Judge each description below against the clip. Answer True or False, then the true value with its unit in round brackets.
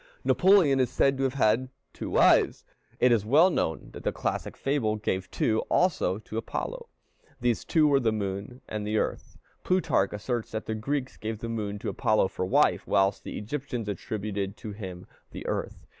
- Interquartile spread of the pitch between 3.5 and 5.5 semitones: True (4.4 semitones)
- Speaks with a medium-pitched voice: False (110 Hz)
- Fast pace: False (185 wpm)